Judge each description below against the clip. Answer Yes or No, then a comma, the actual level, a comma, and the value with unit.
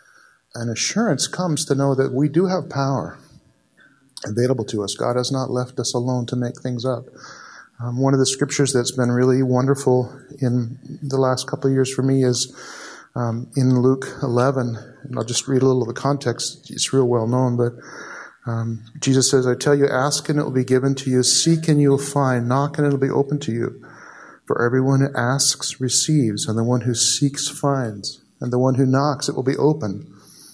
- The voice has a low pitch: Yes, low, 130 Hz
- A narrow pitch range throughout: Yes, narrow, 2.1 semitones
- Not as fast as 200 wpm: No, fast, 205 wpm